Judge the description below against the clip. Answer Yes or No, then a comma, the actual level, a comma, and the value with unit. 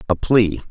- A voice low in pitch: Yes, low, 100 Hz